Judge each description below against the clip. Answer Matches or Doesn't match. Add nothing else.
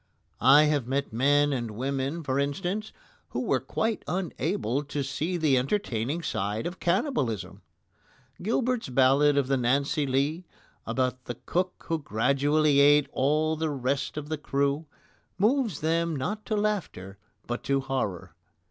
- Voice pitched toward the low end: Doesn't match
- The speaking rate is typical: Matches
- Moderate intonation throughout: Matches